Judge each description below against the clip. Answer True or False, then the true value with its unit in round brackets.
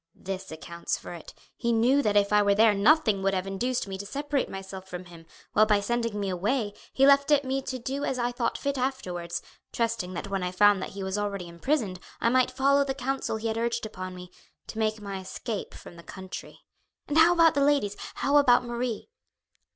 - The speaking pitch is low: False (215 Hz)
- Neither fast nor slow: False (220 wpm)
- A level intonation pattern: False (5.4 semitones)